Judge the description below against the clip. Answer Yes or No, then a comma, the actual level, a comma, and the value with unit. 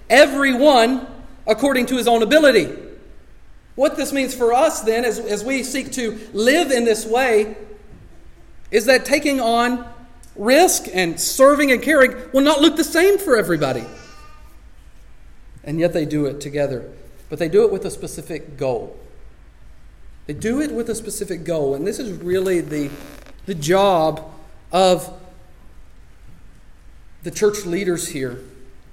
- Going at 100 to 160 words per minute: Yes, average, 145 wpm